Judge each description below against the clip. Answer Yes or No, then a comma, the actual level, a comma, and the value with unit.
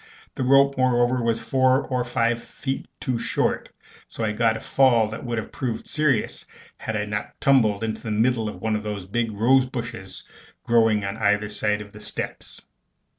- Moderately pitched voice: No, low, 115 Hz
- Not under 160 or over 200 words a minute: Yes, average, 185 wpm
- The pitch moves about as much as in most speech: Yes, average, 3.1 semitones